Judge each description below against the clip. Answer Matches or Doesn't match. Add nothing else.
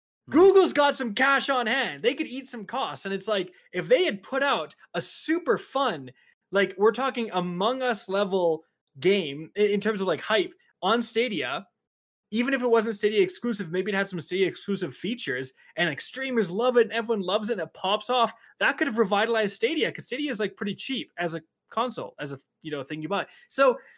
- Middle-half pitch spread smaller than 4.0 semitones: Doesn't match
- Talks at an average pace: Doesn't match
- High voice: Matches